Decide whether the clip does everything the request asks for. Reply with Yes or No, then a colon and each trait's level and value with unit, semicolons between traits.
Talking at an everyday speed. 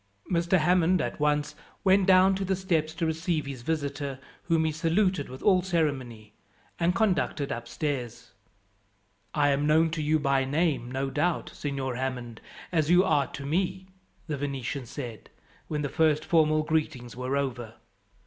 Yes: average, 160 wpm